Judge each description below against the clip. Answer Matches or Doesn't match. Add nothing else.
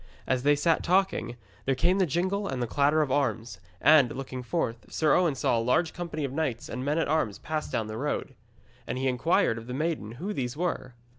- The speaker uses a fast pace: Matches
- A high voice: Doesn't match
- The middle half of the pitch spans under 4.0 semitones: Doesn't match